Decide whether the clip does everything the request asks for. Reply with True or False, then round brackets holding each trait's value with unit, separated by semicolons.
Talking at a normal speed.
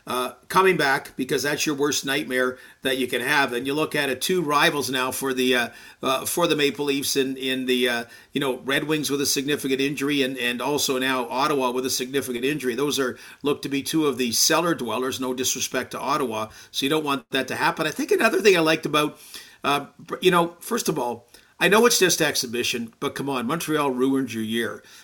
False (230 wpm)